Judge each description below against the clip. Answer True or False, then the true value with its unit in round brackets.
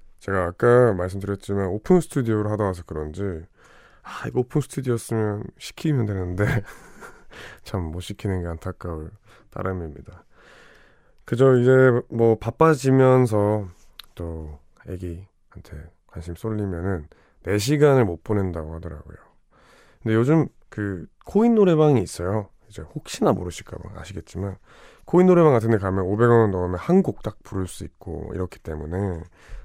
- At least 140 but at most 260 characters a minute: False (300 characters per minute)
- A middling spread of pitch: True (5.0 semitones)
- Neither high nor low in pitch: False (100 Hz)